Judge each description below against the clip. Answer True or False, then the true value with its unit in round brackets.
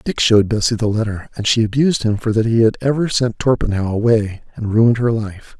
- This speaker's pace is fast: True (225 wpm)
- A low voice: True (110 Hz)